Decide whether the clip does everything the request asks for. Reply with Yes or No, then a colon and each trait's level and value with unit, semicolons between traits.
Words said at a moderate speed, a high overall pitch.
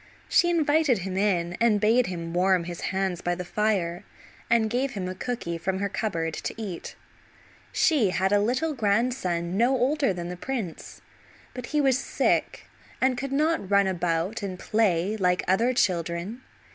Yes: average, 170 wpm; high, 200 Hz